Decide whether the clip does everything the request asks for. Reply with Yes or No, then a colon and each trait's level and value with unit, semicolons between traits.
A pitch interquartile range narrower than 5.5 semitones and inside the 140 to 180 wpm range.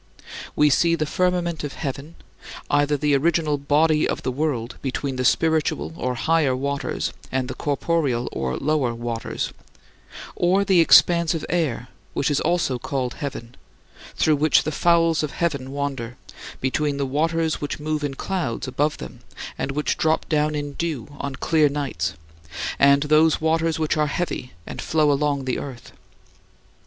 Yes: average, 2.9 semitones; average, 155 wpm